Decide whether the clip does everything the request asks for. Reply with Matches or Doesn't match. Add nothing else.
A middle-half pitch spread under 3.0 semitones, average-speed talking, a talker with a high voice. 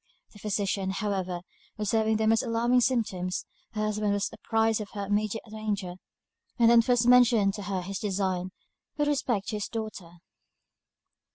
Matches